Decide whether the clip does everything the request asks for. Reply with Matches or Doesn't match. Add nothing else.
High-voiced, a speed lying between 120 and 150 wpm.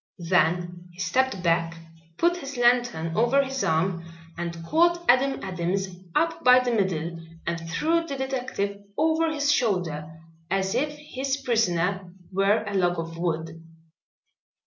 Matches